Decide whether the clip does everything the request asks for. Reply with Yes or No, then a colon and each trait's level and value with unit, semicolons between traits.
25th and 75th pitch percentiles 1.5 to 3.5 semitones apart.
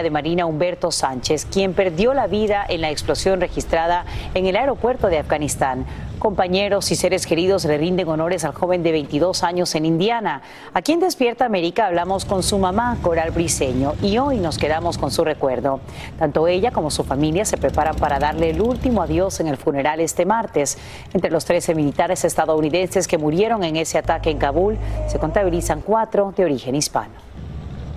No: average, 3.9 semitones